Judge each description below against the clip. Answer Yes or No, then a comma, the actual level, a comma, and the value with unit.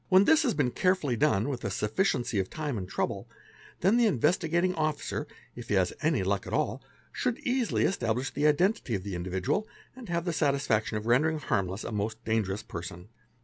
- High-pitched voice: No, medium, 140 Hz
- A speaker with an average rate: Yes, average, 190 wpm